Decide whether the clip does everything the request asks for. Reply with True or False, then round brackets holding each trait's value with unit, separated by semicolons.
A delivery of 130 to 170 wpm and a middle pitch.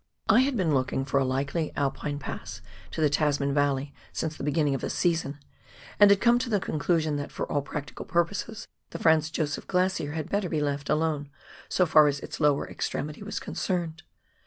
False (195 wpm; 155 Hz)